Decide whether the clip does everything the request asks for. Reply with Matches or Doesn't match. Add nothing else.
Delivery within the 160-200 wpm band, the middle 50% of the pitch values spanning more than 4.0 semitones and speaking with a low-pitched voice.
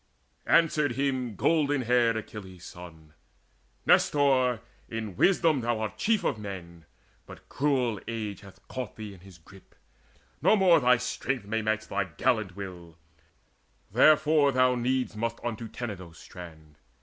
Doesn't match